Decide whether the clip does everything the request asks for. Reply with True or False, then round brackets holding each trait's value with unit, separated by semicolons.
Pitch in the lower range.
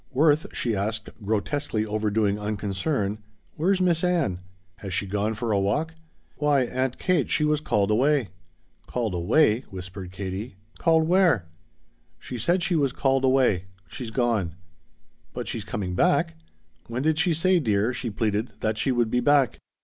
True (115 Hz)